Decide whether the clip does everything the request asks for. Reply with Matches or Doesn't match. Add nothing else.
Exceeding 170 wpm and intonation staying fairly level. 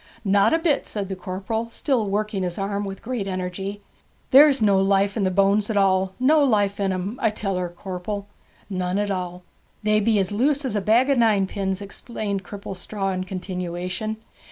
Matches